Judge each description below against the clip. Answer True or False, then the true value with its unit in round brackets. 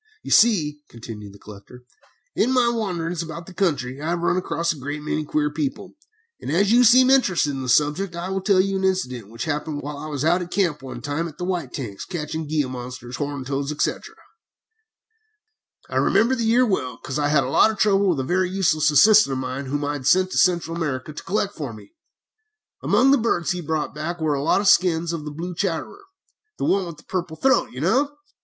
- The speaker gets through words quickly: True (225 wpm)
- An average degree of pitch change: True (4.7 semitones)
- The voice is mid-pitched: True (160 Hz)